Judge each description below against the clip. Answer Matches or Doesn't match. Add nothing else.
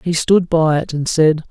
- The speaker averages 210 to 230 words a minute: Doesn't match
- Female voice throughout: Doesn't match